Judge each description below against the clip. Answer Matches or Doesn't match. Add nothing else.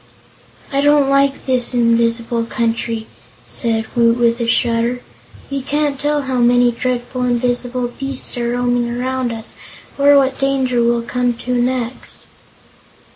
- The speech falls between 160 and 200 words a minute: Doesn't match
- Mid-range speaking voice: Doesn't match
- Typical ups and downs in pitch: Doesn't match